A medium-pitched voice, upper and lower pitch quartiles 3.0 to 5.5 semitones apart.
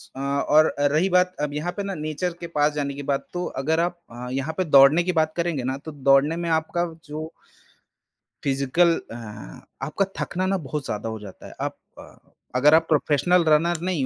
Yes: medium, 155 Hz; average, 3.9 semitones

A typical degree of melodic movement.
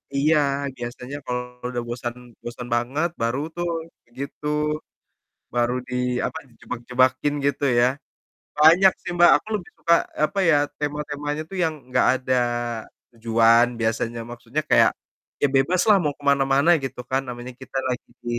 Yes: average, 3.7 semitones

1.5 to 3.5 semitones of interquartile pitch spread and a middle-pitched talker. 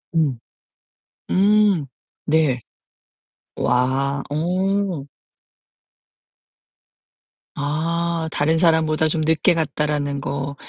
Yes: average, 3.0 semitones; medium, 155 Hz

